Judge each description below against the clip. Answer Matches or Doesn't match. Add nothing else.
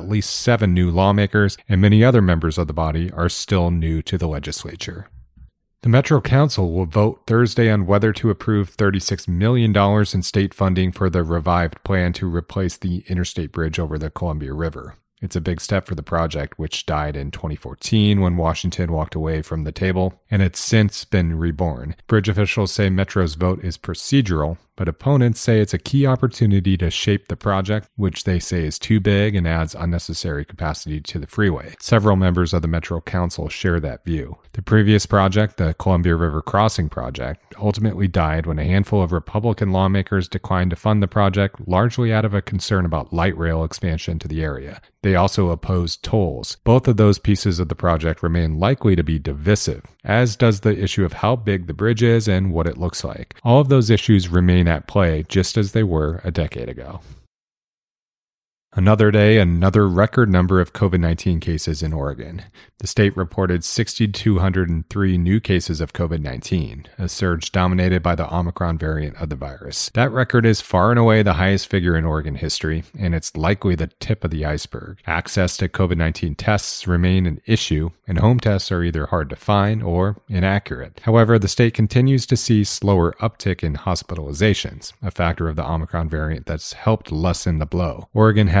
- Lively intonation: Doesn't match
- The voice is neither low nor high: Doesn't match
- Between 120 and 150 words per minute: Doesn't match